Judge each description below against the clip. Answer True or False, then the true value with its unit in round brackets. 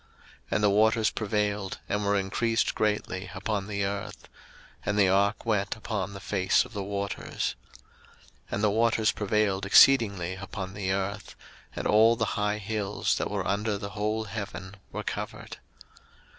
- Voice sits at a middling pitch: False (105 Hz)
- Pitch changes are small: True (1.6 semitones)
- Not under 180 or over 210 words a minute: False (160 wpm)